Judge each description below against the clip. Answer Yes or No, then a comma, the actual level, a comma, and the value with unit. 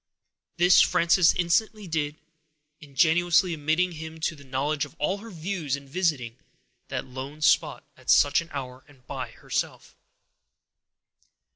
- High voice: No, medium, 155 Hz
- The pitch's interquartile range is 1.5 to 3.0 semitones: No, average, 3.7 semitones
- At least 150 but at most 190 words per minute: No, slow, 135 wpm